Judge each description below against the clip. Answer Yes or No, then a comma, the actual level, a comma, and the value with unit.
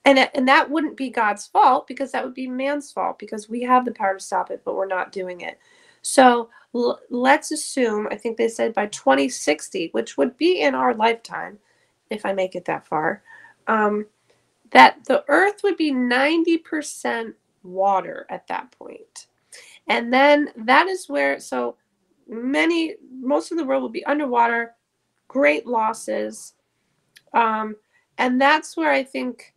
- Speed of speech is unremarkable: Yes, average, 165 wpm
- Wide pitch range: Yes, wide, 5.8 semitones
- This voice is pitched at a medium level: No, very high, 260 Hz